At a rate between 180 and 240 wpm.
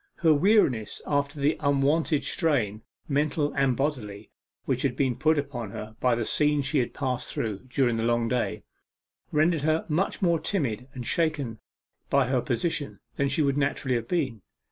No: average, 170 wpm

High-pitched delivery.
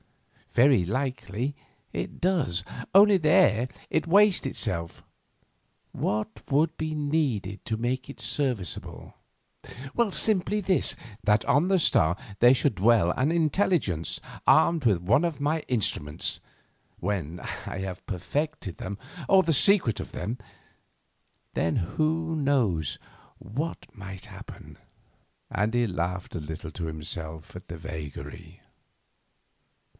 No: low, 115 Hz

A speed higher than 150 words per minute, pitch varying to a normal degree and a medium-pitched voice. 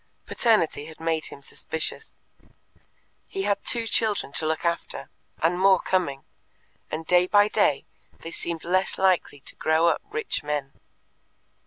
No: average, 145 wpm; average, 3.9 semitones; medium, 170 Hz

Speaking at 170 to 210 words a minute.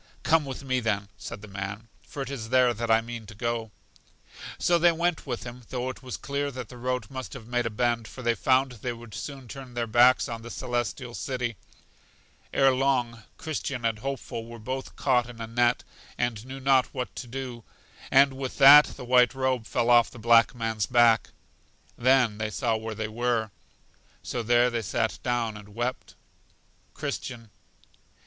Yes: average, 190 wpm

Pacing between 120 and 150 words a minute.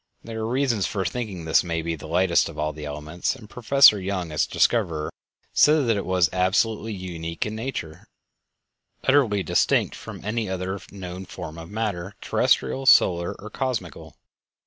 No: average, 170 wpm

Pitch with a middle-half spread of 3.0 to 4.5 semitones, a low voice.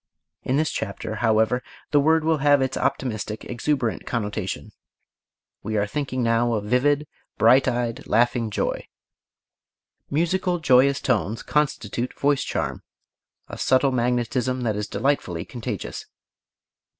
Yes: average, 4.1 semitones; low, 125 Hz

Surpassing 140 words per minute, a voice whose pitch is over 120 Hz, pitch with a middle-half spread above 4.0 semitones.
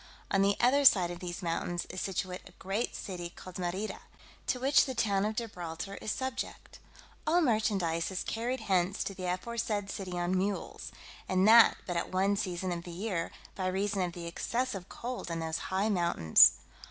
No: average, 185 wpm; high, 190 Hz; average, 3.6 semitones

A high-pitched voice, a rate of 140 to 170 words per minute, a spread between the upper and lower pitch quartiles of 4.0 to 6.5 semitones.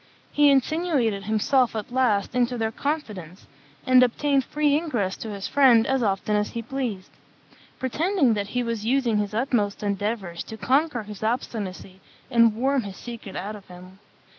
Yes: high, 230 Hz; average, 165 wpm; average, 4.4 semitones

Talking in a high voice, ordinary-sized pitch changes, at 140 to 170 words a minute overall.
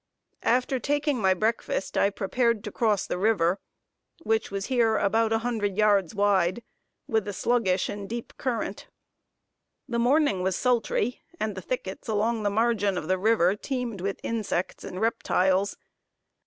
Yes: high, 215 Hz; average, 3.3 semitones; average, 155 wpm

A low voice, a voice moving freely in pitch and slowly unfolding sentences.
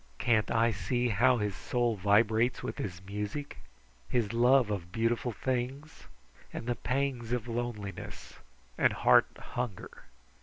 No: low, 115 Hz; average, 2.9 semitones; slow, 130 wpm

